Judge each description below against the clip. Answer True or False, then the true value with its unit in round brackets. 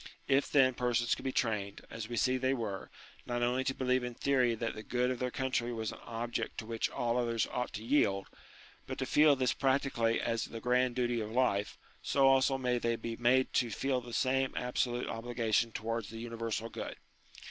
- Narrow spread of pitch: True (2.0 semitones)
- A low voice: True (120 Hz)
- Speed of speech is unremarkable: False (210 wpm)